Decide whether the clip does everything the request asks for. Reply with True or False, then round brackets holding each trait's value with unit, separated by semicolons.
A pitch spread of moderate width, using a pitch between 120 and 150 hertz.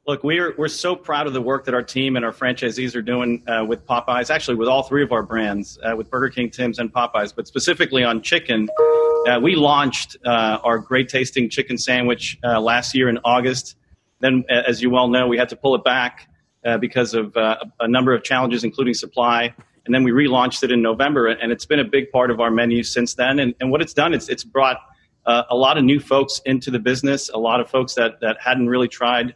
False (2.0 semitones; 125 Hz)